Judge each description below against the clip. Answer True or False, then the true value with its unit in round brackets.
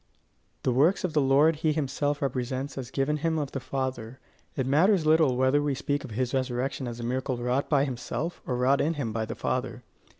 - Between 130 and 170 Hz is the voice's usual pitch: True (135 Hz)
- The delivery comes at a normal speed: False (210 wpm)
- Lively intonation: False (2.6 semitones)